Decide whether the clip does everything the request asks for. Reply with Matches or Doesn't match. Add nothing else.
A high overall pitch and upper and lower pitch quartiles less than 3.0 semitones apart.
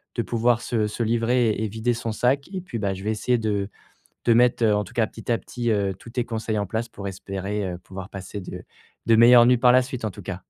Doesn't match